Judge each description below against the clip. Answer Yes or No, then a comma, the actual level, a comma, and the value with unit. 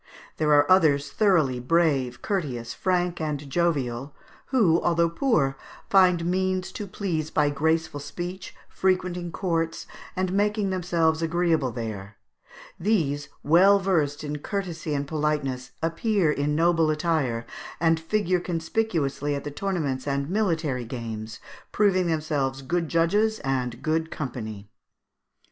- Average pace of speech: No, slow, 125 wpm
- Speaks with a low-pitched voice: No, medium, 160 Hz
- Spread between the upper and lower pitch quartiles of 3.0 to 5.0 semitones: Yes, average, 4.4 semitones